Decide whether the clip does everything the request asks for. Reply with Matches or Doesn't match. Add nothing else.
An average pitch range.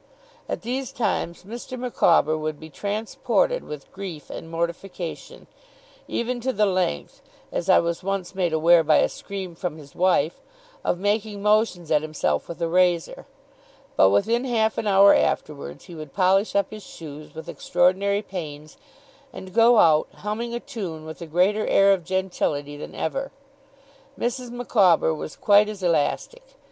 Matches